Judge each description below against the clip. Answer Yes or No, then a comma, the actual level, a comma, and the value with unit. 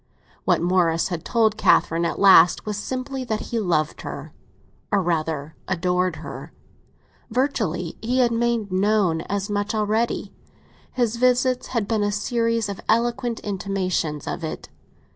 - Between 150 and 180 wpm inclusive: No, average, 140 wpm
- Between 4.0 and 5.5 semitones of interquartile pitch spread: Yes, average, 4.6 semitones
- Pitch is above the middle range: Yes, high, 205 Hz